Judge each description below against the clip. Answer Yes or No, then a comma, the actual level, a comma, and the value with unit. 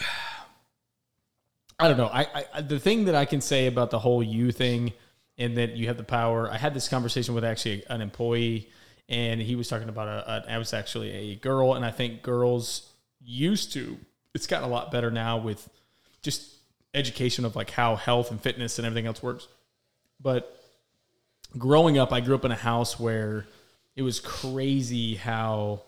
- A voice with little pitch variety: Yes, narrow, 2.1 semitones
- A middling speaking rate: Yes, average, 190 wpm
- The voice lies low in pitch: Yes, low, 120 Hz